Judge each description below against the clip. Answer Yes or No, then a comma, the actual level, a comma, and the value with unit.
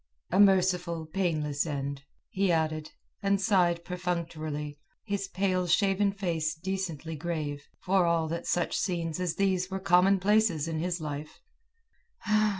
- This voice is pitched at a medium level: Yes, medium, 175 Hz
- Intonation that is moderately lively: Yes, average, 3.3 semitones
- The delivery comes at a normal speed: No, slow, 130 wpm